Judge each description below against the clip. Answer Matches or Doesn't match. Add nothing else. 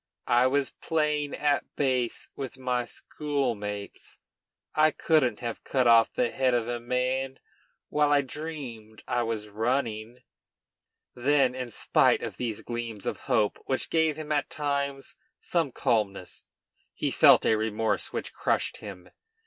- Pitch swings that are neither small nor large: Matches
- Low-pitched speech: Matches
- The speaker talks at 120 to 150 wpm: Matches